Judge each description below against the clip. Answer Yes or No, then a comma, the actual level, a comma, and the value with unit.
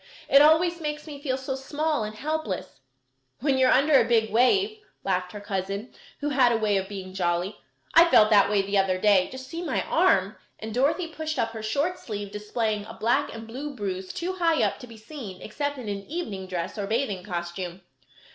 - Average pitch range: No, wide, 6.4 semitones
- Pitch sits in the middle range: No, high, 225 Hz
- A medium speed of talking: No, fast, 210 wpm